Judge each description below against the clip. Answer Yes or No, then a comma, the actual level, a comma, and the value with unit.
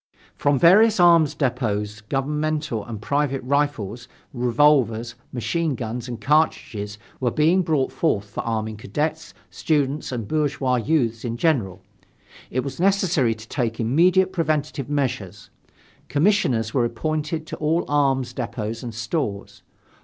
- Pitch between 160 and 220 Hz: No, low, 135 Hz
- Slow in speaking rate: Yes, slow, 130 wpm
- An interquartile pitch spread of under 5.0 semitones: No, average, 5.3 semitones